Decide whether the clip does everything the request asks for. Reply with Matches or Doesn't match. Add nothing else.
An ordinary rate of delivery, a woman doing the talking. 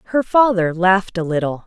Matches